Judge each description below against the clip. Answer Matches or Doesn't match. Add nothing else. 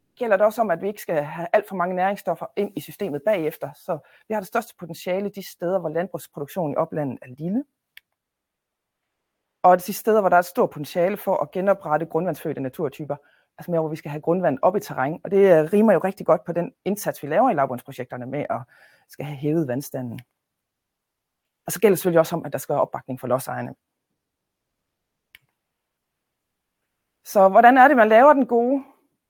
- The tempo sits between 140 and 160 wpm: Doesn't match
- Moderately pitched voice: Matches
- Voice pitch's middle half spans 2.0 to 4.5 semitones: Doesn't match